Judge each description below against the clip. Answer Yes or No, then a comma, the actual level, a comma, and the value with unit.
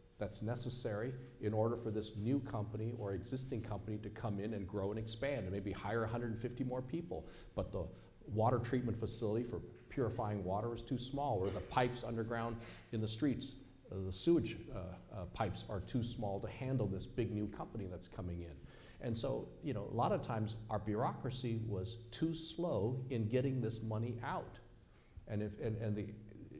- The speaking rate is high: No, average, 185 wpm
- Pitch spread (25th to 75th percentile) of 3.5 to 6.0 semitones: No, average, 2.9 semitones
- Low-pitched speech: Yes, low, 110 Hz